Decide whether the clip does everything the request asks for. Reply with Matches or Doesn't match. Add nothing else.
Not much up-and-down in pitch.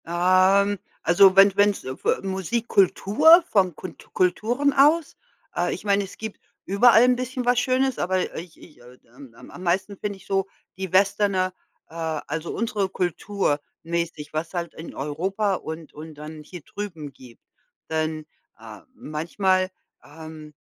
Doesn't match